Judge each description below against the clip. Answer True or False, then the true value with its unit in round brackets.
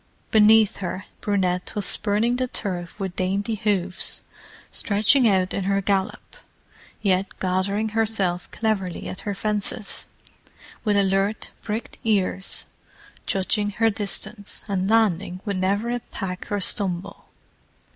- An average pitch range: False (2.3 semitones)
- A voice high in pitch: True (200 Hz)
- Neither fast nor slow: False (120 wpm)